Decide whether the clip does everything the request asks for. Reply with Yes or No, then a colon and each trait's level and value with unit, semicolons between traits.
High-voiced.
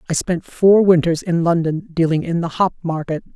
No: medium, 170 Hz